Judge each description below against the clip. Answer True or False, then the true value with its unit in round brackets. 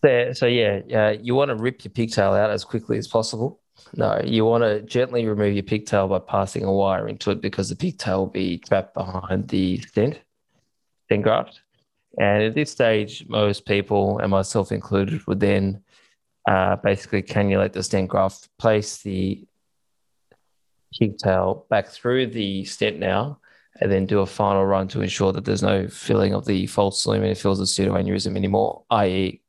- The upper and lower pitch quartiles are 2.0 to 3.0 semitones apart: True (2.4 semitones)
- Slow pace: False (180 wpm)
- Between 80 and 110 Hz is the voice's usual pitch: True (100 Hz)